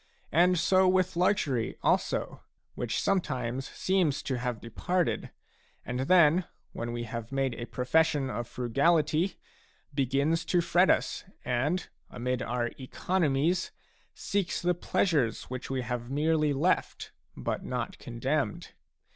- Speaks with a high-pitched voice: No, medium, 140 Hz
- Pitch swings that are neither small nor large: No, wide, 5.9 semitones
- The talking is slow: Yes, slow, 125 wpm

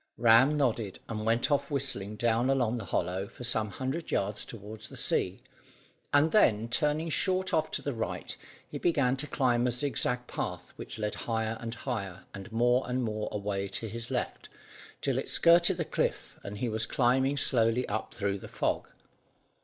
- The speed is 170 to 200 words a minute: Yes, average, 180 wpm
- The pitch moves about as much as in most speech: Yes, average, 4.0 semitones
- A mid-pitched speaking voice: No, low, 120 Hz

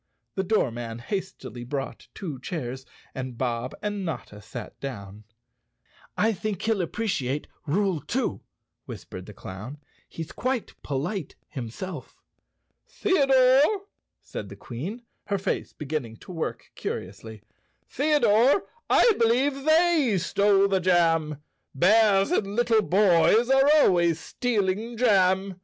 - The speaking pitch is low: No, medium, 185 Hz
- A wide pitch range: Yes, wide, 9.0 semitones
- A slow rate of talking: Yes, slow, 115 wpm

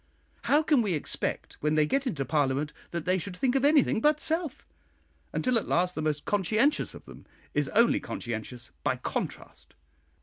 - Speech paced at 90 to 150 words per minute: No, average, 175 wpm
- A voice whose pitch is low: No, medium, 185 Hz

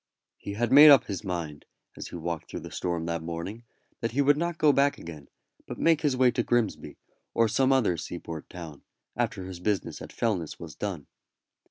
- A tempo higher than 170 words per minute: Yes, average, 200 wpm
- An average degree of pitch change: No, wide, 7.5 semitones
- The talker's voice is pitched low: Yes, low, 100 Hz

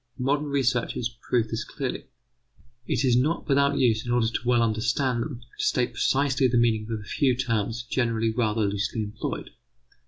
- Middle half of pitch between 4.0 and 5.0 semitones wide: No, average, 2.7 semitones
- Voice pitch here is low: Yes, low, 120 Hz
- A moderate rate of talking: Yes, average, 175 wpm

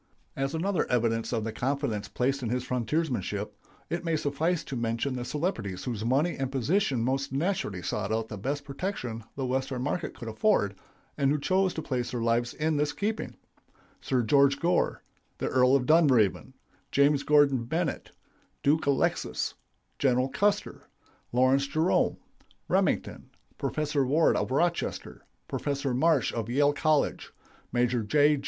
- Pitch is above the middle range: No, low, 135 Hz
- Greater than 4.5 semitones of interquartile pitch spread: No, average, 3.9 semitones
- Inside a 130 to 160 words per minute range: Yes, average, 145 wpm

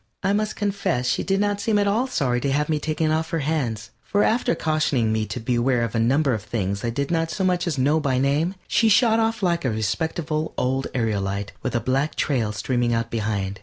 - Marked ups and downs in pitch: Yes, wide, 6.7 semitones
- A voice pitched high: No, medium, 140 Hz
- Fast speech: Yes, fast, 230 wpm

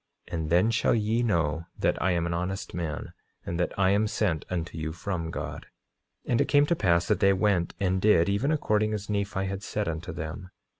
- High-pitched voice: No, very low, 95 Hz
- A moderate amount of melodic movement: Yes, average, 3.8 semitones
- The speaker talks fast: Yes, fast, 215 wpm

